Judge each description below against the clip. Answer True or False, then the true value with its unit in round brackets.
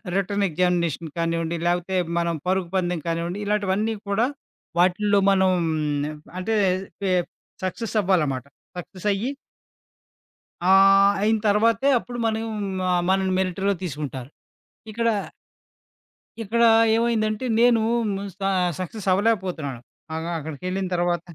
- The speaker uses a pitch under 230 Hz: True (190 Hz)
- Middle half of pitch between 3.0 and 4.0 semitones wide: True (3.4 semitones)